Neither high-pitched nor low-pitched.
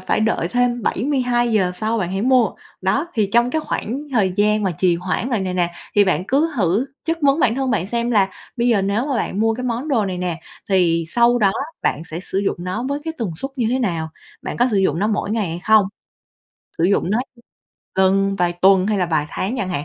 No: high, 210 Hz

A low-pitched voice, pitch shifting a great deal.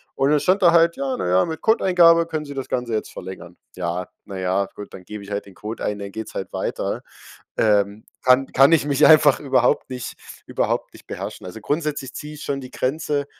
Yes: low, 130 Hz; wide, 6.9 semitones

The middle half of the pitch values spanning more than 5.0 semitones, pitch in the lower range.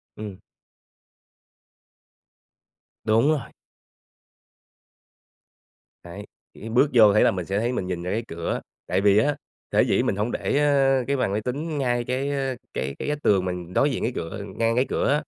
Yes: wide, 5.6 semitones; low, 115 Hz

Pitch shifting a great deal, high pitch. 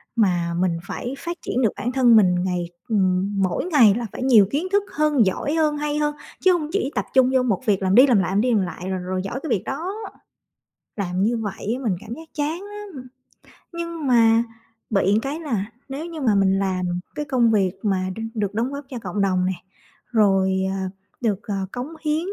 Yes: wide, 7.0 semitones; high, 230 Hz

